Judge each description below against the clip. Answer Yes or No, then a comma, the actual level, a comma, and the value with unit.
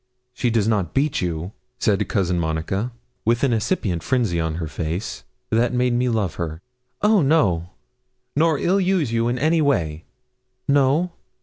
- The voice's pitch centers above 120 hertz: No, low, 115 Hz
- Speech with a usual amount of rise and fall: No, wide, 8.2 semitones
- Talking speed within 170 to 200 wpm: No, average, 160 wpm